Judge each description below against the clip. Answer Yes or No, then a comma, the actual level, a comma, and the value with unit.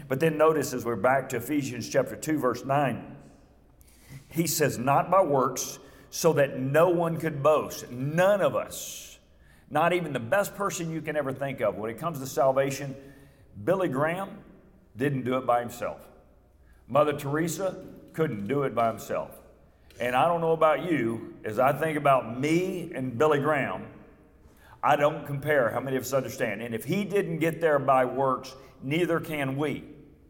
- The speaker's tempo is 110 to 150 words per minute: No, average, 175 wpm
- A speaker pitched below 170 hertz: Yes, medium, 140 Hz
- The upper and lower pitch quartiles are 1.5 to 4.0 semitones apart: Yes, average, 3.5 semitones